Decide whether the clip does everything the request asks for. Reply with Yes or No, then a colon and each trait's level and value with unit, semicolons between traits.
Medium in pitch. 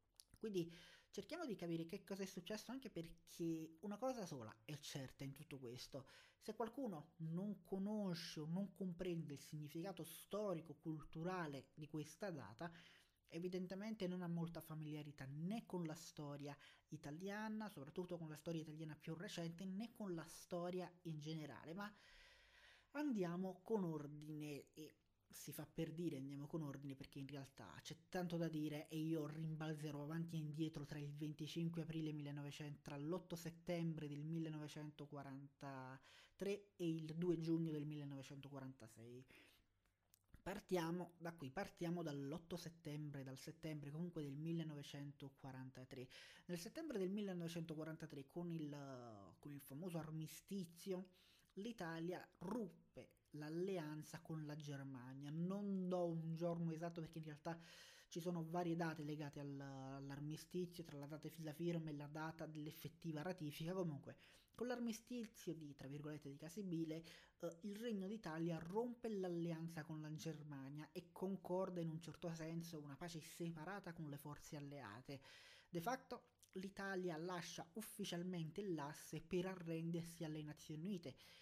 Yes: medium, 160 Hz